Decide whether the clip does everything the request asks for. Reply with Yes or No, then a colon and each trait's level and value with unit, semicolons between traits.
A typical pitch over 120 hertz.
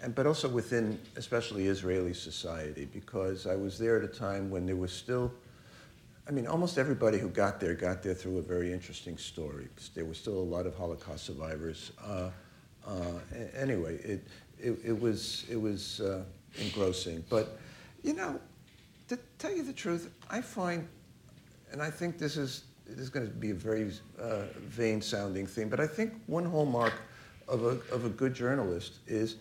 No: low, 110 Hz